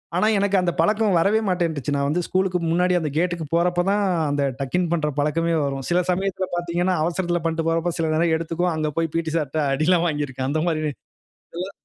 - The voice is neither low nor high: Yes, medium, 170 Hz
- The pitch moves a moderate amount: No, narrow, 2.3 semitones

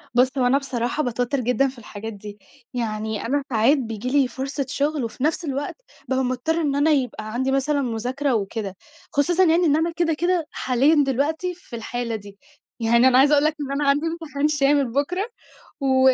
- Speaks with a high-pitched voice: Yes, very high, 270 Hz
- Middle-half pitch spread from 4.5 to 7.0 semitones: No, average, 3.5 semitones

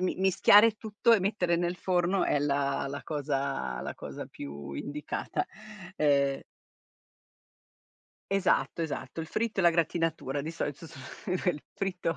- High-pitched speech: No, medium, 165 Hz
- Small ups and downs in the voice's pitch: No, average, 4.6 semitones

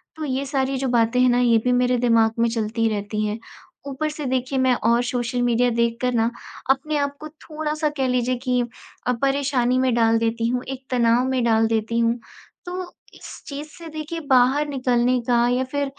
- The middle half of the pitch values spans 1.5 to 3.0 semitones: Yes, average, 2.7 semitones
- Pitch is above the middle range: Yes, very high, 250 Hz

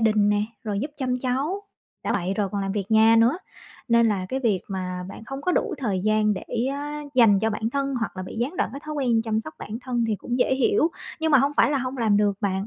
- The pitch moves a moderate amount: Yes, average, 4.3 semitones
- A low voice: No, high, 225 Hz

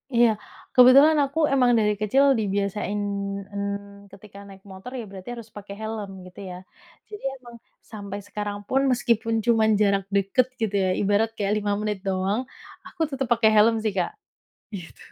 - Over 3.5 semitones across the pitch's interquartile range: No, average, 2.8 semitones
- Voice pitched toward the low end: No, high, 210 Hz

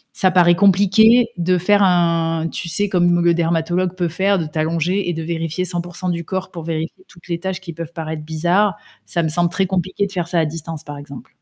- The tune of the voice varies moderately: No, narrow, 2.1 semitones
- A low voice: No, medium, 175 Hz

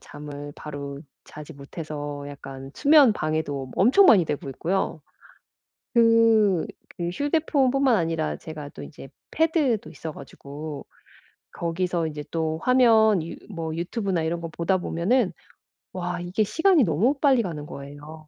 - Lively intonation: Yes, wide, 7.1 semitones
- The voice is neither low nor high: Yes, medium, 170 Hz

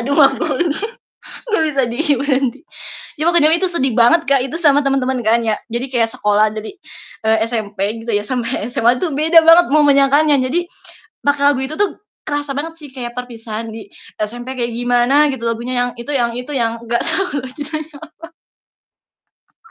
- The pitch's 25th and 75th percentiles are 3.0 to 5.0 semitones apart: Yes, average, 3.8 semitones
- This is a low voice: No, very high, 260 Hz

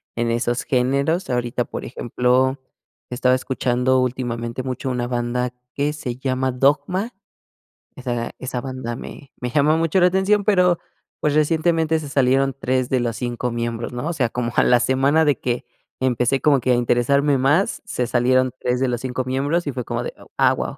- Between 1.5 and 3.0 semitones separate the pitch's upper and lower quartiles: Yes, average, 2.7 semitones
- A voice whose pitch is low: Yes, low, 130 Hz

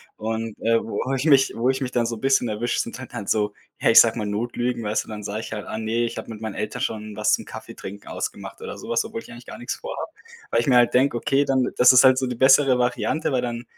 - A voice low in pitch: Yes, low, 120 Hz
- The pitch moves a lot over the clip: No, average, 2.8 semitones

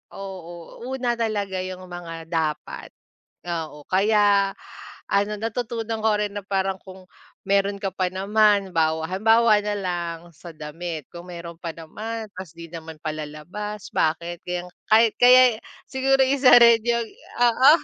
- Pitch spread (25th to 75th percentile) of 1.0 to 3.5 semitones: No, average, 4.4 semitones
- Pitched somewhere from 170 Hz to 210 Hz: Yes, high, 190 Hz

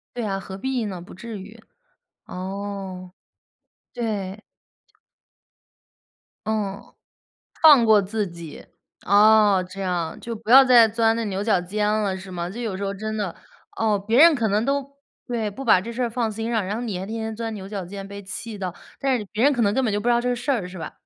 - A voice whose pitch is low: No, high, 210 Hz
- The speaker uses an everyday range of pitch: Yes, average, 3.1 semitones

